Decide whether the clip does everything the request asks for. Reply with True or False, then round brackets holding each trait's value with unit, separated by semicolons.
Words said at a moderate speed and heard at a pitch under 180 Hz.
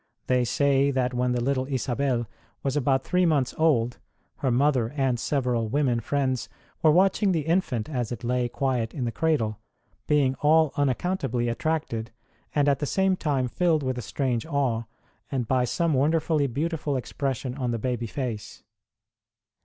True (160 wpm; 135 Hz)